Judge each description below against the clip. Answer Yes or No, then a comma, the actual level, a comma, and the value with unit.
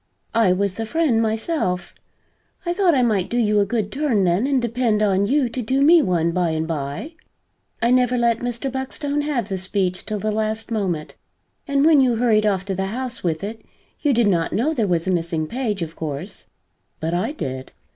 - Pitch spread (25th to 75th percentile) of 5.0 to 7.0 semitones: Yes, wide, 5.6 semitones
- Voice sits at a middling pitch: No, high, 220 Hz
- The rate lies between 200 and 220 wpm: Yes, fast, 205 wpm